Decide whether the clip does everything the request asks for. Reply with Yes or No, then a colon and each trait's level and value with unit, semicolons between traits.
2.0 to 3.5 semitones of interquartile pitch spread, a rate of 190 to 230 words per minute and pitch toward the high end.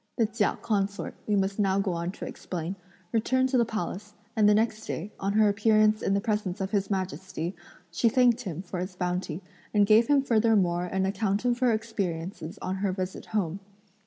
Yes: average, 2.8 semitones; average, 195 wpm; high, 200 Hz